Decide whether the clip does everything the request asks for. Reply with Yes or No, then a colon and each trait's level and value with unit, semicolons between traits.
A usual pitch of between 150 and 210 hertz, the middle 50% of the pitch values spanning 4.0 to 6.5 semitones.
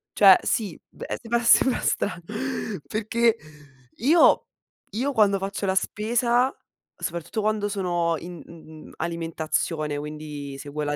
Yes: medium, 185 Hz; wide, 5.4 semitones